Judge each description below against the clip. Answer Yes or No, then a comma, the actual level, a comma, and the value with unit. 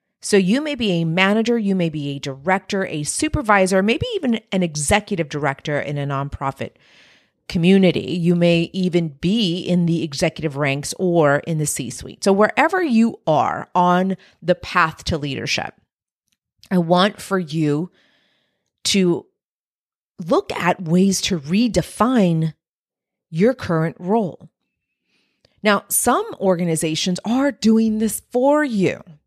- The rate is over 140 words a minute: No, slow, 135 wpm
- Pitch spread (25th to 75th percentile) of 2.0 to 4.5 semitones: Yes, average, 4.0 semitones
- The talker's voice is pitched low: No, medium, 180 Hz